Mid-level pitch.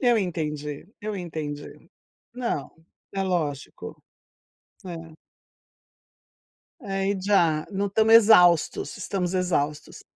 Yes: medium, 180 Hz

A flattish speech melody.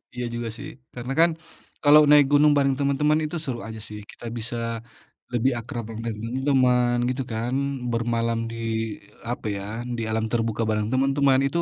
No: average, 3.1 semitones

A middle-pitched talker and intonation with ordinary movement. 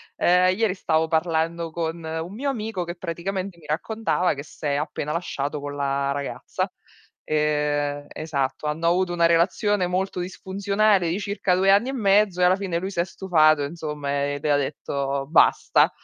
Yes: medium, 170 Hz; average, 4.0 semitones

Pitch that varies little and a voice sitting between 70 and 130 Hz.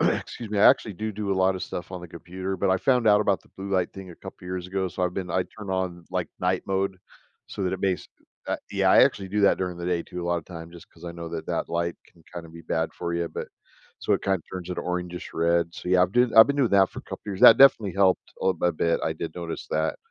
Yes: narrow, 2.1 semitones; very low, 90 Hz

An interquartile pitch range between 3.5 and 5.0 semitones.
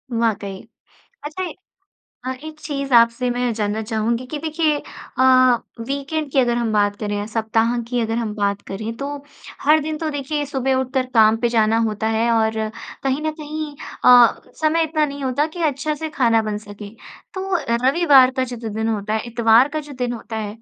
Yes: average, 4.6 semitones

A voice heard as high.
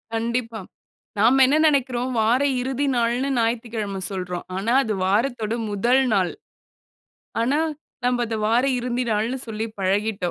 Yes: high, 230 Hz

